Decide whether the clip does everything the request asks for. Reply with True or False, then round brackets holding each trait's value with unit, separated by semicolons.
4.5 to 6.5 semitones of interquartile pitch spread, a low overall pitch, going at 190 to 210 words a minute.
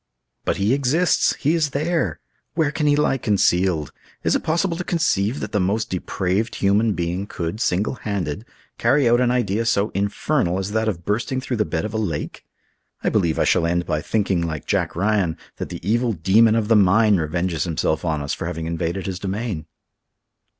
True (5.1 semitones; 100 Hz; 195 wpm)